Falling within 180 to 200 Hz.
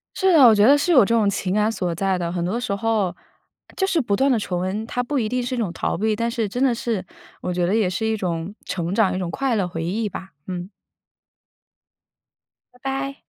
No: high, 215 Hz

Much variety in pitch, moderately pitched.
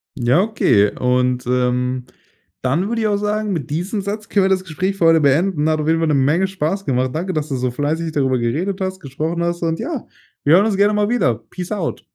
Yes: wide, 6.4 semitones; medium, 165 Hz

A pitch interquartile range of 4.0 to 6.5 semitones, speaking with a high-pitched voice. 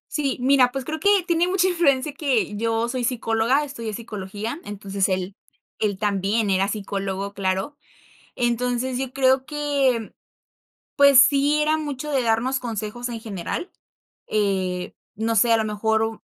Yes: average, 4.7 semitones; high, 235 Hz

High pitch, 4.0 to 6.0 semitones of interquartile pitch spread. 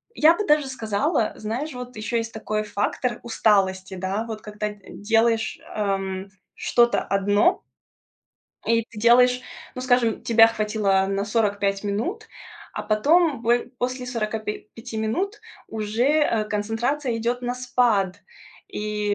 No: high, 225 Hz; average, 3.0 semitones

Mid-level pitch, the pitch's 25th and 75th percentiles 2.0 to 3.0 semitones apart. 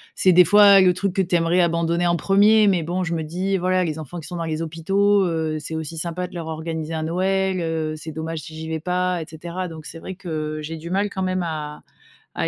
Yes: medium, 170 Hz; narrow, 2.5 semitones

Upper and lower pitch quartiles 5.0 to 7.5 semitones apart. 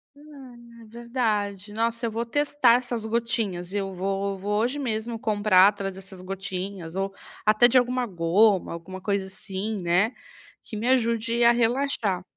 No: average, 3.4 semitones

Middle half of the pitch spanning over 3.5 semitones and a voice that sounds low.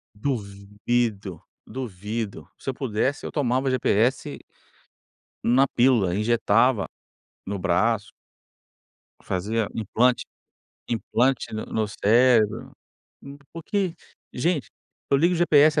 Yes: average, 4.1 semitones; low, 115 Hz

